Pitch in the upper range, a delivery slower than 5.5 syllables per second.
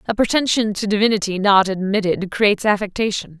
No: high, 205 Hz; 5.9 syllables/s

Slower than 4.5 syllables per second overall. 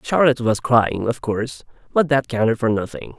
No: 5.4 syllables/s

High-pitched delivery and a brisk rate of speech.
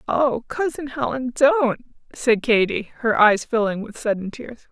No: high, 240 Hz; average, 155 wpm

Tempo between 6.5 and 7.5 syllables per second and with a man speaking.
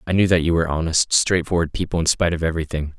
Yes: 7.4 syllables/s; male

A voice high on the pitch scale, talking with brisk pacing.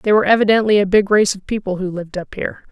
Yes: high, 200 Hz; fast, 265 wpm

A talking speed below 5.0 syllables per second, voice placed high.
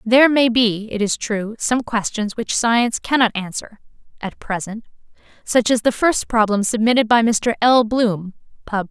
Yes: 4.6 syllables/s; high, 225 Hz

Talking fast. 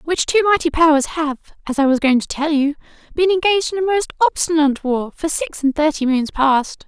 Yes: fast, 220 wpm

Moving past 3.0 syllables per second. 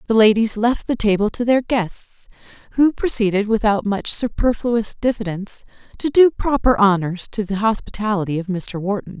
Yes: 5.0 syllables/s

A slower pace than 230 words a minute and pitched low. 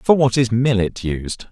Yes: average, 200 wpm; low, 115 Hz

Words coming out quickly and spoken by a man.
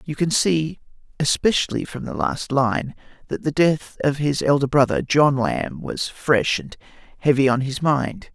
No: average, 170 wpm; male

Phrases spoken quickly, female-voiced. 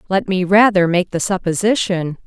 No: average, 160 wpm; female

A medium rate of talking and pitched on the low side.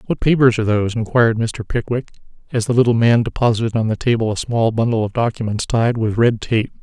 No: fast, 210 wpm; low, 115 Hz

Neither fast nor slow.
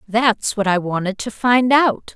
Yes: average, 195 wpm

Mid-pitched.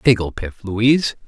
No: low, 115 Hz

